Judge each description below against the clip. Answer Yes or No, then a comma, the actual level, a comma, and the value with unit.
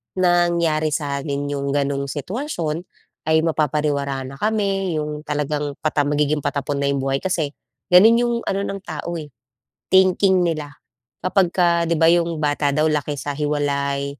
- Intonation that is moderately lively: Yes, average, 3.4 semitones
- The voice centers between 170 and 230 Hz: No, medium, 150 Hz